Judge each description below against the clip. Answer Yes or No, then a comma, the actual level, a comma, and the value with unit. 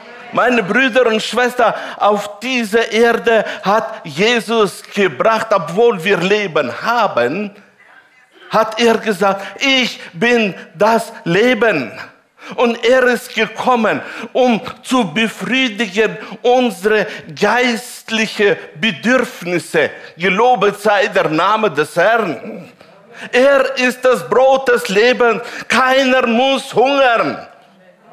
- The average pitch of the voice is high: Yes, high, 225 Hz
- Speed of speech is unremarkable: No, slow, 100 wpm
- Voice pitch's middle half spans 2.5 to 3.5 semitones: Yes, average, 3.1 semitones